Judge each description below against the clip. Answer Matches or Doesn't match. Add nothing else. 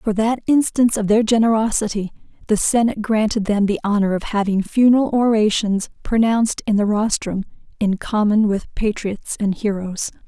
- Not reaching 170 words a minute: Matches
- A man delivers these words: Doesn't match